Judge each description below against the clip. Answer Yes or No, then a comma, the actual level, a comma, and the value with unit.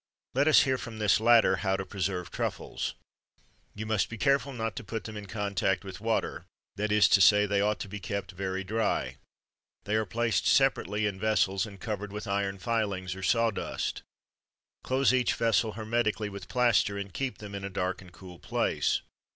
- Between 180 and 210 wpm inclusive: Yes, average, 195 wpm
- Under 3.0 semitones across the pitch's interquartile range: Yes, narrow, 2.5 semitones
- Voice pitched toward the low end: Yes, low, 105 Hz